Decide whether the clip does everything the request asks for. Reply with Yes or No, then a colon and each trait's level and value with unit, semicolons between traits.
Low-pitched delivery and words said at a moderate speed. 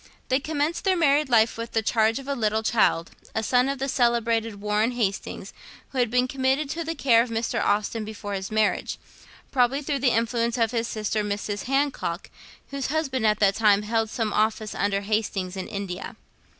No: high, 230 Hz; average, 190 wpm